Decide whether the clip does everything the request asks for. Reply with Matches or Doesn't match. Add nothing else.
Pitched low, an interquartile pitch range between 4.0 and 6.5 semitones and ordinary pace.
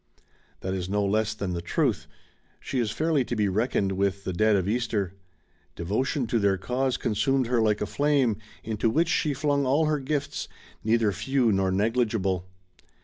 Matches